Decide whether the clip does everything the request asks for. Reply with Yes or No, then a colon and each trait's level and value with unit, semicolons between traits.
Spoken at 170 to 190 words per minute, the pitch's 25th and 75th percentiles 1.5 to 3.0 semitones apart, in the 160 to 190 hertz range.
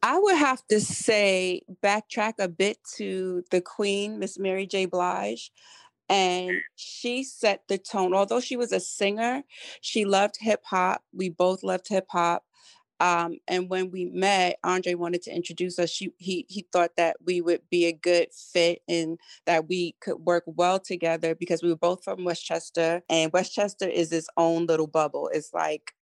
Yes: average, 175 wpm; average, 2.7 semitones; medium, 185 Hz